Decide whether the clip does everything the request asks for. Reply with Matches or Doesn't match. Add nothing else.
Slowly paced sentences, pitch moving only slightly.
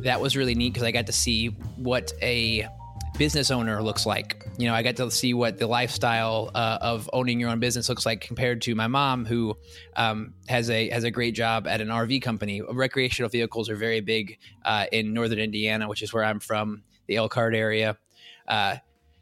Doesn't match